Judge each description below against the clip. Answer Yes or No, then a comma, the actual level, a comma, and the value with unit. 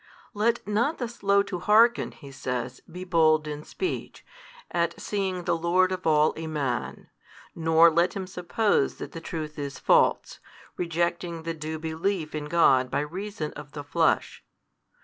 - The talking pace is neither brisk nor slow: Yes, average, 160 wpm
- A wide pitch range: No, average, 3.5 semitones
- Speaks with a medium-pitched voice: Yes, medium, 165 Hz